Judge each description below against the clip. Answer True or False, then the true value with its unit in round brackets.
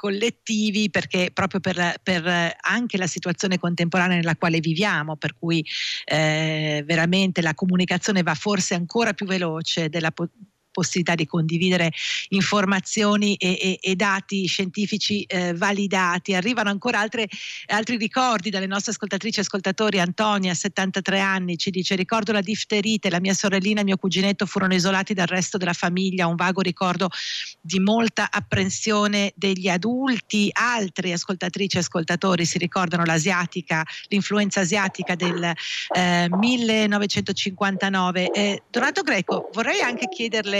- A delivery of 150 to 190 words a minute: False (135 wpm)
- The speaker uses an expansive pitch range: False (2.6 semitones)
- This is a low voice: False (190 Hz)